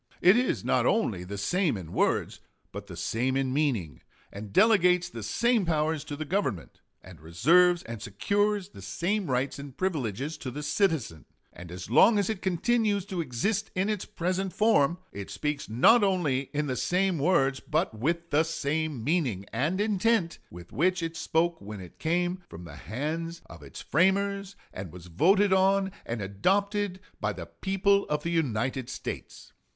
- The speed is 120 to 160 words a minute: No, average, 175 wpm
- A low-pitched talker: No, medium, 160 Hz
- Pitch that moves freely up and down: Yes, wide, 8.5 semitones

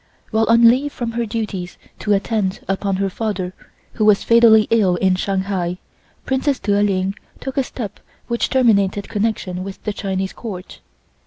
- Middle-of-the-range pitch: No, high, 205 Hz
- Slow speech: No, average, 160 wpm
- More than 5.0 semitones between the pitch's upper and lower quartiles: No, average, 3.2 semitones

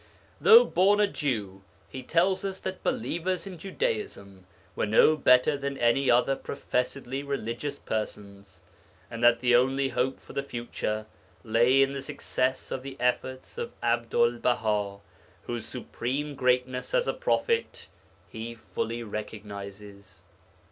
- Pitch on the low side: Yes, low, 125 Hz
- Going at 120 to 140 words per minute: Yes, slow, 135 wpm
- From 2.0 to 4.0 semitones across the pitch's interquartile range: No, average, 4.7 semitones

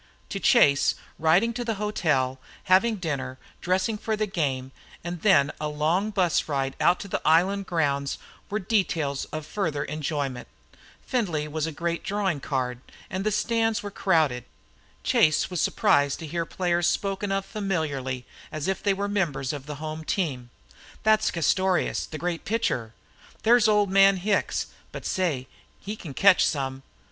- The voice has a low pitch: No, medium, 170 Hz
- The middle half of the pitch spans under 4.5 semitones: No, wide, 5.5 semitones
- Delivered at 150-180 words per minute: Yes, average, 160 wpm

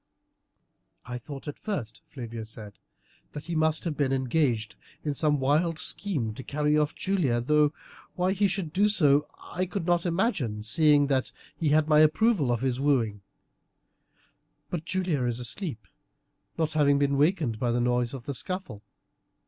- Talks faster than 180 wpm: No, average, 165 wpm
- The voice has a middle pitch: Yes, medium, 145 Hz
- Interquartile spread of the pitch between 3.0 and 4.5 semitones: No, average, 5.2 semitones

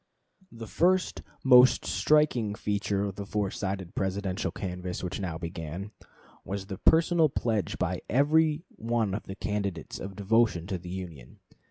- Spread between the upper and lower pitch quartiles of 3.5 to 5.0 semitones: Yes, average, 4.0 semitones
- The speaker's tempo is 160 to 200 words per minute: No, average, 150 wpm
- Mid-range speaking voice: No, low, 100 Hz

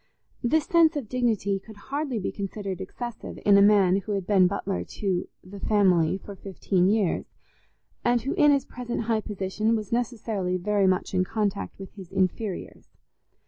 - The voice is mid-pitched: No, high, 205 Hz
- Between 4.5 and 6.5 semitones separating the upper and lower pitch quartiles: No, average, 3.5 semitones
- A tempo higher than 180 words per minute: No, average, 170 wpm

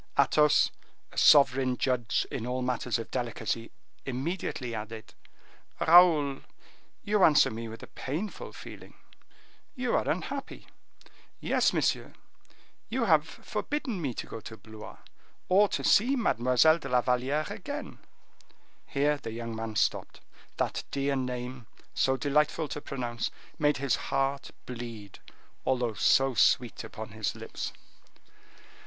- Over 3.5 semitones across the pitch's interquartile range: Yes, average, 4.1 semitones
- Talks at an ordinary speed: No, slow, 130 wpm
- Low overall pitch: Yes, low, 130 Hz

